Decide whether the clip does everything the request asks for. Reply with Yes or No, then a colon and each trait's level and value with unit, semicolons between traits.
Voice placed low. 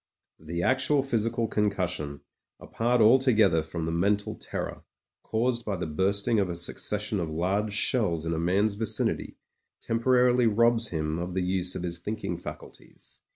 Yes: low, 100 Hz